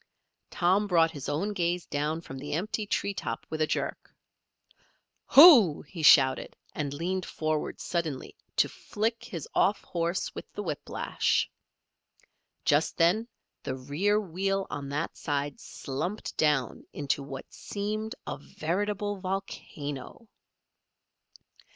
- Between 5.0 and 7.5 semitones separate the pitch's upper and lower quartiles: Yes, wide, 5.5 semitones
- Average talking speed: No, slow, 125 wpm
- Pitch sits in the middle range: Yes, medium, 170 Hz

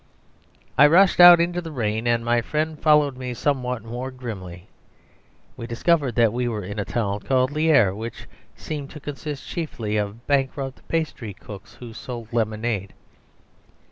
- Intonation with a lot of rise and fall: No, average, 4.8 semitones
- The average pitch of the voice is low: Yes, low, 125 Hz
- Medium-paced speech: Yes, average, 150 wpm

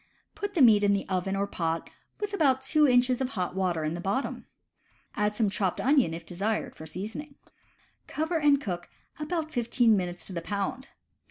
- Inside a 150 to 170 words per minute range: No, average, 185 wpm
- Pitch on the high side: Yes, high, 210 Hz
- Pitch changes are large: Yes, wide, 6.9 semitones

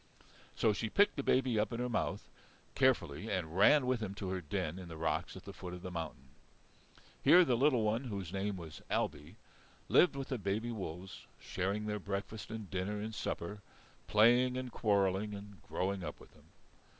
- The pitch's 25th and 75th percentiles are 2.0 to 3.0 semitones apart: No, average, 4.1 semitones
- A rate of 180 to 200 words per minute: Yes, average, 190 wpm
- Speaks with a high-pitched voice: No, low, 105 Hz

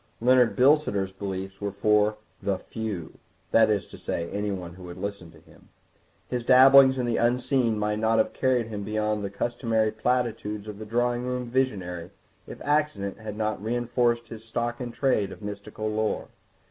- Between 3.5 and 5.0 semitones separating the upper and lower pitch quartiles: No, average, 3.0 semitones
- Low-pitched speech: Yes, low, 110 Hz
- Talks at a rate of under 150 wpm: No, average, 170 wpm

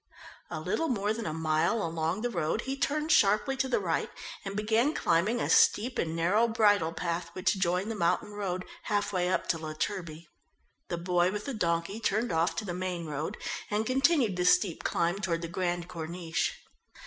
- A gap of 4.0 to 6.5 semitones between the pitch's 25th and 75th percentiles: Yes, average, 4.3 semitones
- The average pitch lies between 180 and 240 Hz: Yes, medium, 185 Hz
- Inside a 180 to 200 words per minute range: Yes, average, 195 wpm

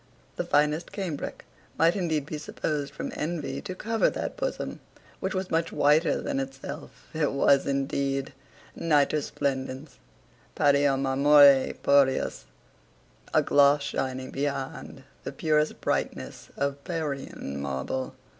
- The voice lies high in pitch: No, medium, 145 Hz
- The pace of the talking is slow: Yes, slow, 120 wpm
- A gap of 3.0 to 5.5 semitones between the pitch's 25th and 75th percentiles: No, narrow, 2.4 semitones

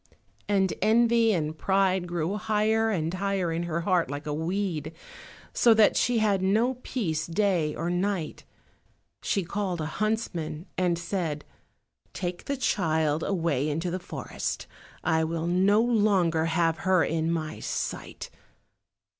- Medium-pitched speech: Yes, medium, 180 Hz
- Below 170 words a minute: Yes, average, 140 wpm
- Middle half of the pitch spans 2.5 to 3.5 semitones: No, average, 4.0 semitones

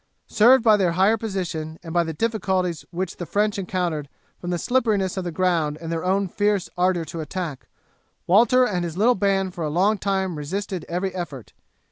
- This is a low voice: No, medium, 185 Hz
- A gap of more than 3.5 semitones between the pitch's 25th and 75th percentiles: No, average, 3.0 semitones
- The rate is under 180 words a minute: No, average, 190 wpm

